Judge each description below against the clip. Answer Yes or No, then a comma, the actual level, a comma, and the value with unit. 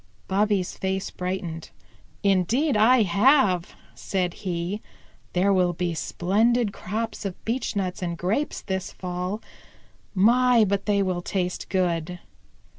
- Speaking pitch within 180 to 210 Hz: Yes, high, 190 Hz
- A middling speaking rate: No, slow, 115 wpm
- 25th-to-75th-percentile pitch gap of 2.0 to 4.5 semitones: Yes, average, 3.0 semitones